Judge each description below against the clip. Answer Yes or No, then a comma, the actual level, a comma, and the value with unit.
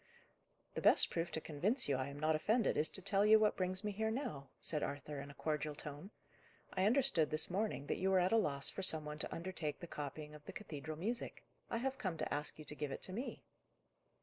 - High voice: No, medium, 165 Hz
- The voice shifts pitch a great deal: Yes, wide, 5.7 semitones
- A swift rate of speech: Yes, fast, 240 wpm